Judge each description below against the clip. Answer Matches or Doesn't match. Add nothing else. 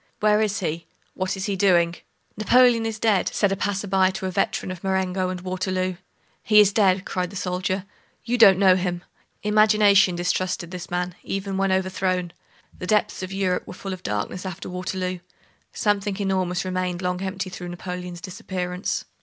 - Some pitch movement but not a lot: Doesn't match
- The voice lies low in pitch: Doesn't match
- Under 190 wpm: Matches